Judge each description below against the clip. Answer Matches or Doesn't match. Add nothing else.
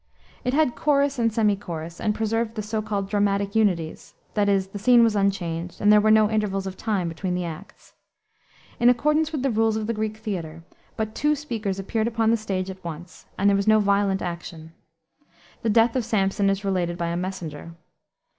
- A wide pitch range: Doesn't match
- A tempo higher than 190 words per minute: Matches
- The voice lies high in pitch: Matches